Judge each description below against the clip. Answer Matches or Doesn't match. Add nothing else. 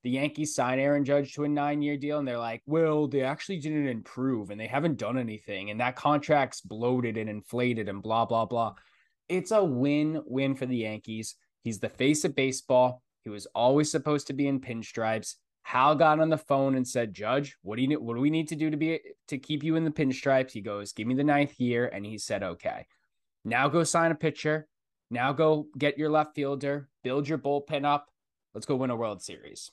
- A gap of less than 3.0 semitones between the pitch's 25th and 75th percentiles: Doesn't match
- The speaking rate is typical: Doesn't match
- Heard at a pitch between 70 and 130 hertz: Doesn't match